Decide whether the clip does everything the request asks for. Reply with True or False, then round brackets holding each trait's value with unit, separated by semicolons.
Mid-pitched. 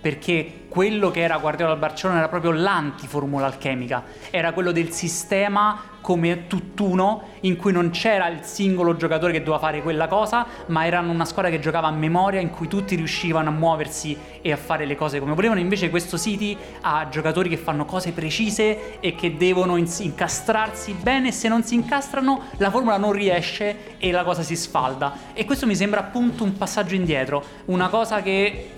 True (175 Hz)